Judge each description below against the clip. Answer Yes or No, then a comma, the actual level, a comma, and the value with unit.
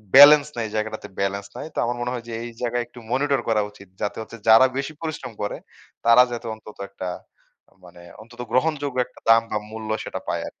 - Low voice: Yes, low, 120 Hz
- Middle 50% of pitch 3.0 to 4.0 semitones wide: Yes, average, 3.5 semitones